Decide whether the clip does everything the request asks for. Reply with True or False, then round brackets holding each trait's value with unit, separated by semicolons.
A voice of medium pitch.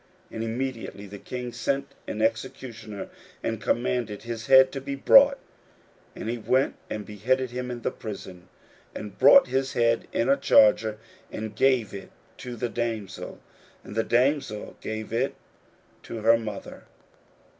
False (115 Hz)